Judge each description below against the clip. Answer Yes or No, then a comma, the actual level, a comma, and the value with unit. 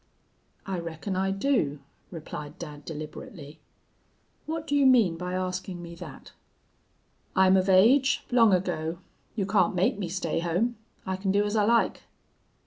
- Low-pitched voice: No, medium, 185 Hz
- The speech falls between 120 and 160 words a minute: Yes, average, 150 wpm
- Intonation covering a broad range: No, average, 3.6 semitones